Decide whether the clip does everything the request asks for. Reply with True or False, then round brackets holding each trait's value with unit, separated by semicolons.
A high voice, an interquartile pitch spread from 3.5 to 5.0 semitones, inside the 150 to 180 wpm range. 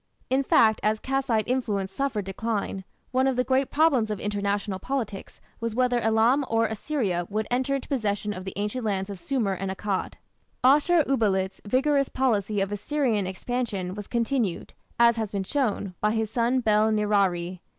True (220 Hz; 4.2 semitones; 170 wpm)